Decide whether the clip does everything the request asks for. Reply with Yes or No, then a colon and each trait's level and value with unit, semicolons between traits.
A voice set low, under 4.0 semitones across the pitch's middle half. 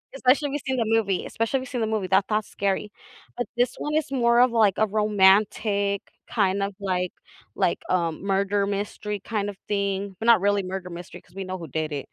No: high, 200 Hz; average, 2.8 semitones